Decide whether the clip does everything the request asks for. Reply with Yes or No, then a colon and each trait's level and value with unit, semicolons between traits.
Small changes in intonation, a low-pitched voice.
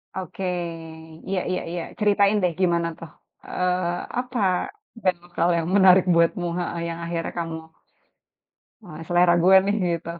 No: narrow, 2.0 semitones; medium, 175 Hz